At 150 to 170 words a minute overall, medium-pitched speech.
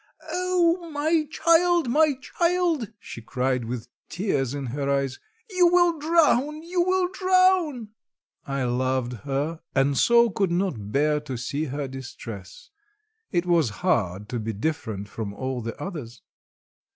No: average, 140 wpm; medium, 165 Hz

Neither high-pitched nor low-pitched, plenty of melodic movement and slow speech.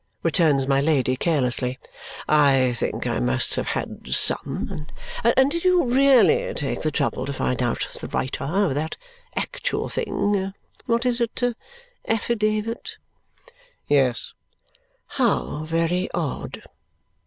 Yes: medium, 160 Hz; wide, 8.8 semitones; slow, 120 wpm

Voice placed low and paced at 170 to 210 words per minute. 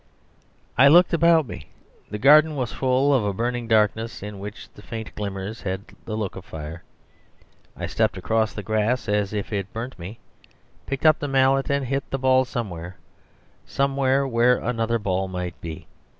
Yes: low, 115 Hz; average, 175 wpm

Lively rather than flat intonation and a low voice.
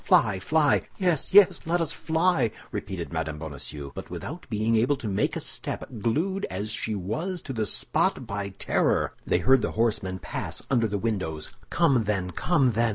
Yes: wide, 7.0 semitones; low, 110 Hz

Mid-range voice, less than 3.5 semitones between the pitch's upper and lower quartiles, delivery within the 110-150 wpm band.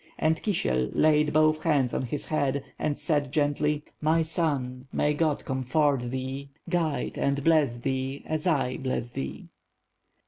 Yes: medium, 145 Hz; average, 2.9 semitones; average, 145 wpm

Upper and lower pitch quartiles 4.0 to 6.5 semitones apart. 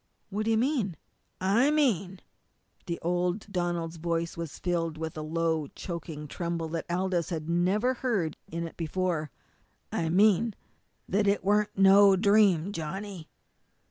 No: average, 3.4 semitones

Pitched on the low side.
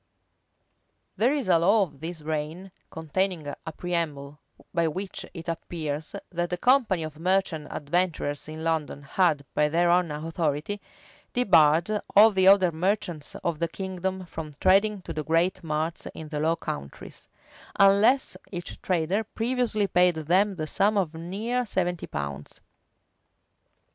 No: medium, 175 Hz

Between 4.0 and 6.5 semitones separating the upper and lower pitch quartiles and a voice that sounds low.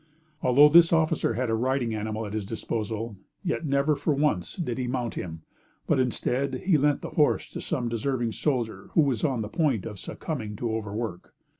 Yes: average, 4.5 semitones; low, 125 Hz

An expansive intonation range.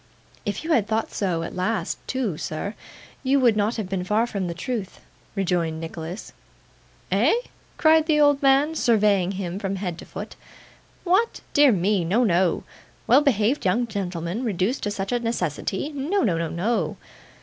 Yes: wide, 5.7 semitones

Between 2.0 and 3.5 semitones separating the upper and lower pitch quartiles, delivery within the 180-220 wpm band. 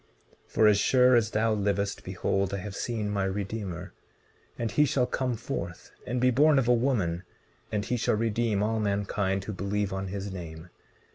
Yes: average, 3.2 semitones; average, 190 wpm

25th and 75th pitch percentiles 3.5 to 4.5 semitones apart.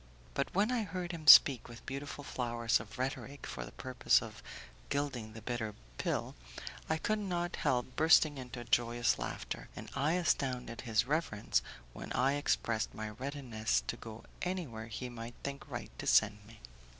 Yes: average, 4.2 semitones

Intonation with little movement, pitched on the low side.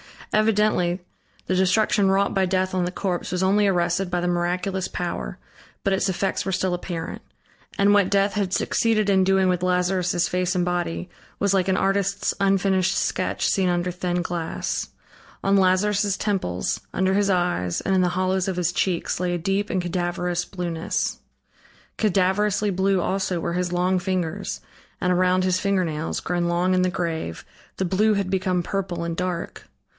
No: narrow, 1.7 semitones; medium, 185 Hz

